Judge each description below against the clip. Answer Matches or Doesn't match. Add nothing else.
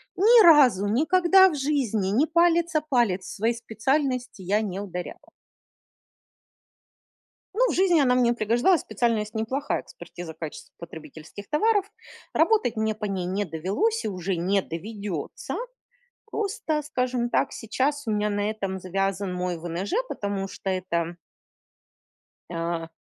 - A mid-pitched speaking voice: Doesn't match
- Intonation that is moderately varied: Doesn't match